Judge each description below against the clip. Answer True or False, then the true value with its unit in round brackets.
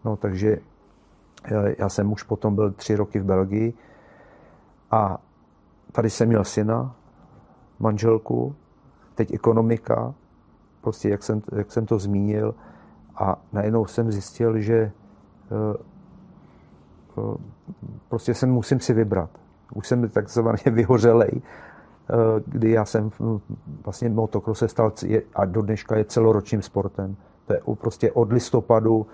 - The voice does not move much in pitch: True (2.1 semitones)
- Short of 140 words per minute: True (115 wpm)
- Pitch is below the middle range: True (110 Hz)